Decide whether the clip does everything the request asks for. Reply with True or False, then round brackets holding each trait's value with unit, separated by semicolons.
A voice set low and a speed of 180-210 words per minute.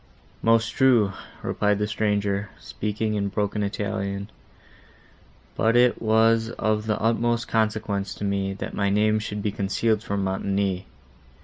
False (105 Hz; 135 wpm)